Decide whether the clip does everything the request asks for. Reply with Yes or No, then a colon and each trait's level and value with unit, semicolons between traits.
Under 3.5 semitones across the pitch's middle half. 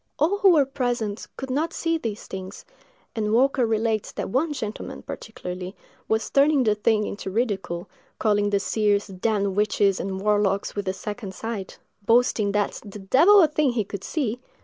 No: average, 4.2 semitones